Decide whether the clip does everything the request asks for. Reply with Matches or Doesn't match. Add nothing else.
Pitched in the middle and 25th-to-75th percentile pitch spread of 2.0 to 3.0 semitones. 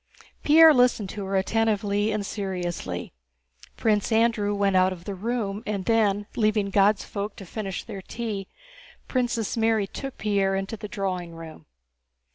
Doesn't match